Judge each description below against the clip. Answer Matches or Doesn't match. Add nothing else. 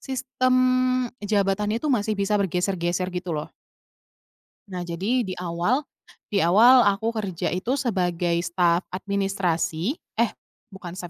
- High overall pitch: Matches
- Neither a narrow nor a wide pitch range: Matches